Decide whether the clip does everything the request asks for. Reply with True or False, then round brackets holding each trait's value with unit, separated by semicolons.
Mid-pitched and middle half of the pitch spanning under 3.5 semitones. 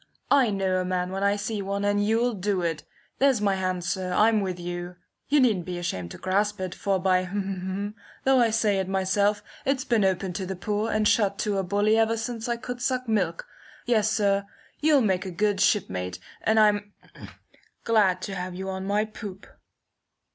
False (200 Hz; 2.8 semitones)